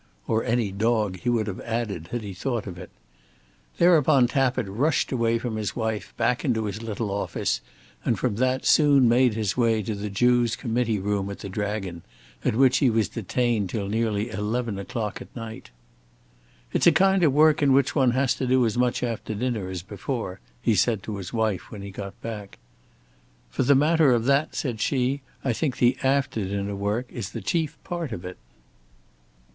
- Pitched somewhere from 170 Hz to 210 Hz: No, low, 115 Hz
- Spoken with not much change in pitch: No, average, 3.8 semitones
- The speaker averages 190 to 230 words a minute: Yes, average, 195 wpm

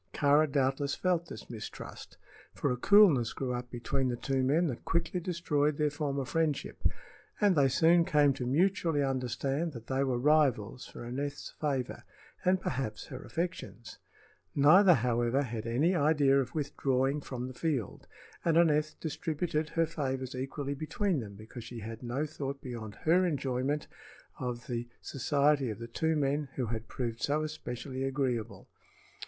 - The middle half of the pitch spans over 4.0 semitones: No, average, 3.7 semitones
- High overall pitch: No, medium, 140 Hz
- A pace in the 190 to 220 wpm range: No, average, 160 wpm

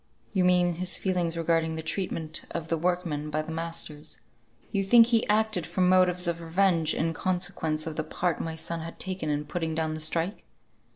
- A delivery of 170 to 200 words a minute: Yes, average, 190 wpm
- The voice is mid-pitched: Yes, medium, 170 Hz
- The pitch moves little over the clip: Yes, narrow, 2.3 semitones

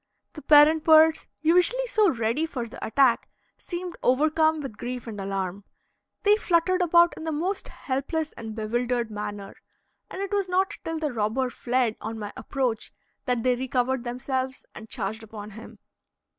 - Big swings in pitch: Yes, wide, 6.2 semitones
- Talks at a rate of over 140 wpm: Yes, average, 165 wpm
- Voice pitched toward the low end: No, very high, 260 Hz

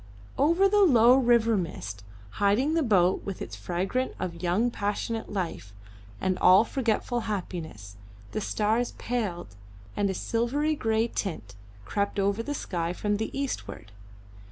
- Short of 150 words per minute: Yes, average, 140 wpm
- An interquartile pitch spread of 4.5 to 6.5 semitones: Yes, average, 5.0 semitones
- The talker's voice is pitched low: No, high, 210 Hz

